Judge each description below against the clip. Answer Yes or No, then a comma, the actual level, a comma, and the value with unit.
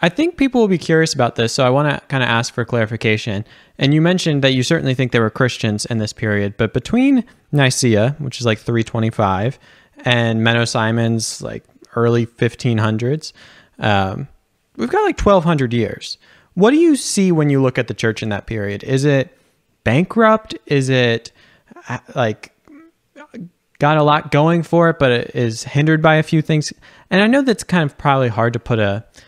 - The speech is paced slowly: No, average, 190 wpm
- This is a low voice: Yes, low, 130 Hz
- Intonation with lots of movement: Yes, wide, 5.9 semitones